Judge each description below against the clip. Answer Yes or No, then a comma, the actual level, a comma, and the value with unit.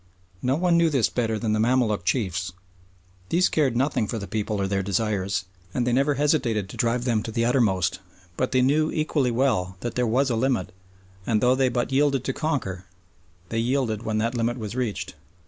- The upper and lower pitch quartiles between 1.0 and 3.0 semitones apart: No, average, 3.8 semitones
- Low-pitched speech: Yes, low, 120 Hz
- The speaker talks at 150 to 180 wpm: No, average, 200 wpm